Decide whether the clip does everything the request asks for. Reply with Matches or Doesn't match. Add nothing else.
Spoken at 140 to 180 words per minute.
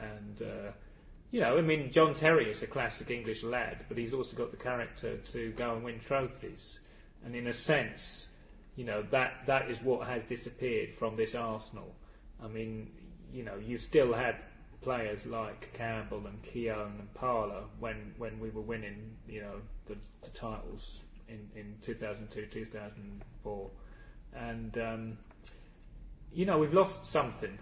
Matches